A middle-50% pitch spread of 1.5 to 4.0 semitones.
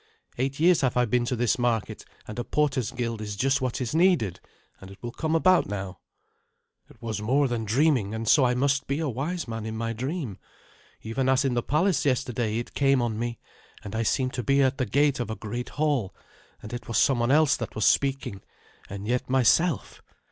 Yes: average, 3.6 semitones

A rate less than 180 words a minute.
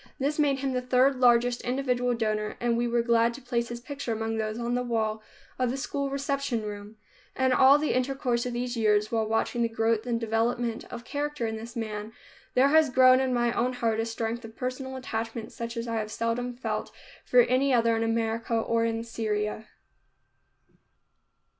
No: average, 195 wpm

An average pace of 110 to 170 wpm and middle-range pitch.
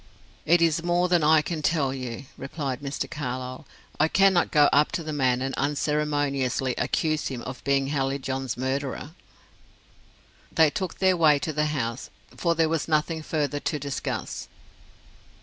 Yes: average, 155 wpm; medium, 145 Hz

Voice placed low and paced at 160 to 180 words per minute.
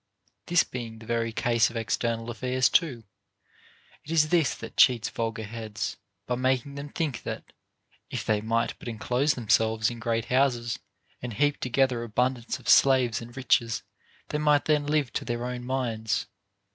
Yes: low, 120 Hz; average, 165 wpm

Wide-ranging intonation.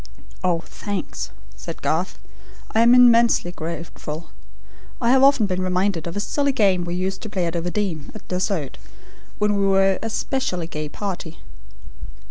No: average, 3.8 semitones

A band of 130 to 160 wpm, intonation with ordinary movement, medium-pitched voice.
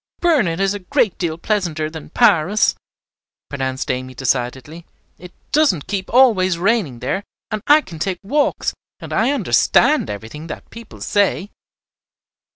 No: average, 140 wpm; wide, 6.0 semitones; medium, 180 Hz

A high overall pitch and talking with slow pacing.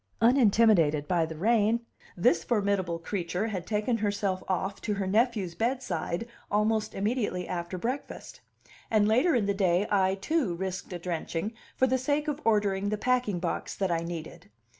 No: high, 200 Hz; average, 160 wpm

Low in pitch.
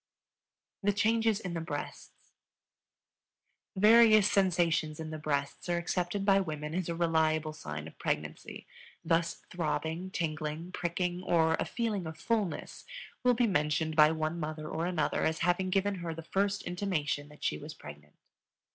No: medium, 170 Hz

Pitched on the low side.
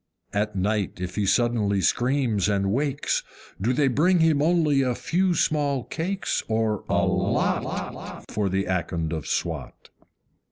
Yes: low, 115 Hz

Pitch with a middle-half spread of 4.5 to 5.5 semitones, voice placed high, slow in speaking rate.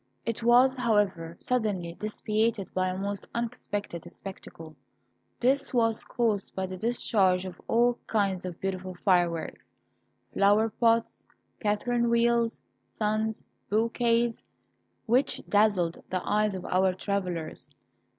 No: average, 3.8 semitones; high, 210 Hz; slow, 110 wpm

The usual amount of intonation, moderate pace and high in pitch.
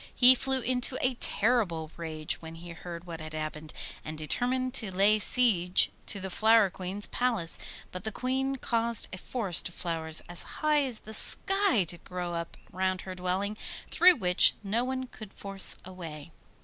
No: wide, 6.2 semitones; average, 175 wpm; high, 195 Hz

